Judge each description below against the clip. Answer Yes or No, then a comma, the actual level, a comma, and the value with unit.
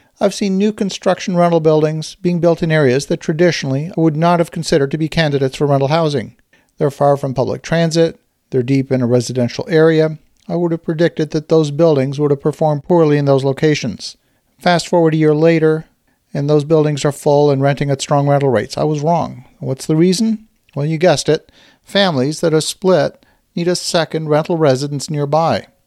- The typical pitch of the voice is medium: Yes, medium, 155 Hz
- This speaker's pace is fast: No, average, 195 wpm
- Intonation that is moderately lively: Yes, average, 3.1 semitones